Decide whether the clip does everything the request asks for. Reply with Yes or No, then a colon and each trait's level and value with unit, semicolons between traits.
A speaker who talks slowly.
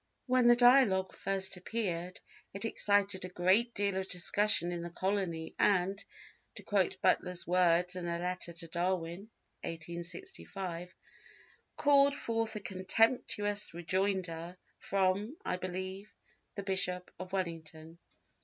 Yes: slow, 125 wpm